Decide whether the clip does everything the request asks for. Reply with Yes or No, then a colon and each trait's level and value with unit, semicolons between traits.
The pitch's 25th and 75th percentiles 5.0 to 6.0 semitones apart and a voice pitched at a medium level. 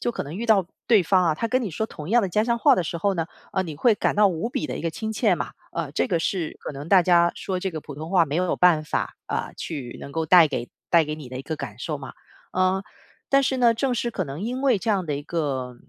Yes: wide, 5.6 semitones; medium, 175 Hz